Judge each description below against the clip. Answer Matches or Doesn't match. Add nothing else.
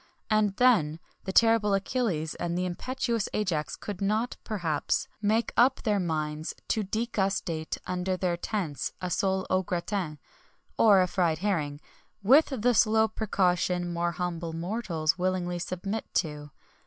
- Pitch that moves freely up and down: Doesn't match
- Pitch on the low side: Doesn't match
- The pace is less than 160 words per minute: Matches